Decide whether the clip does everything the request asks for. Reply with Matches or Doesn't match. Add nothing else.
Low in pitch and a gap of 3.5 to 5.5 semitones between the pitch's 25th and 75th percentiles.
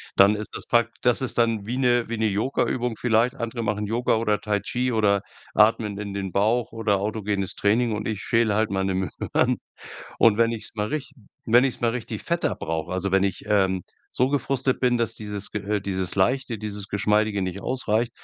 Doesn't match